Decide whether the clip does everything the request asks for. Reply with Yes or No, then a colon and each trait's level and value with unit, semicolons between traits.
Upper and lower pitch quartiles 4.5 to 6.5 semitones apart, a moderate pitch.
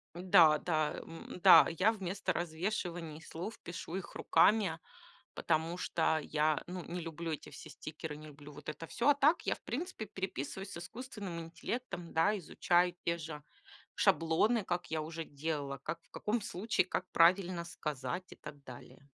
No: average, 3.5 semitones; medium, 170 Hz